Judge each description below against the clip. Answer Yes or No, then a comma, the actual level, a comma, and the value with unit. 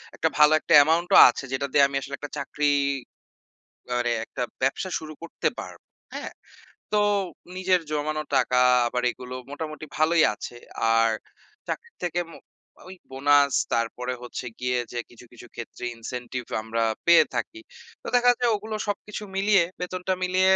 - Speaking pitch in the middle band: Yes, medium, 145 Hz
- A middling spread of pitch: No, wide, 6.3 semitones